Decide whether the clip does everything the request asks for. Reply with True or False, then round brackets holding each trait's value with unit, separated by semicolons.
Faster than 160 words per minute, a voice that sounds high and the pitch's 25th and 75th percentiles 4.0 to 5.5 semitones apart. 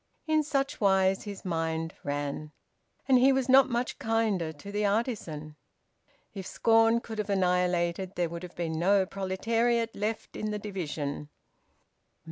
False (145 wpm; 195 Hz; 4.8 semitones)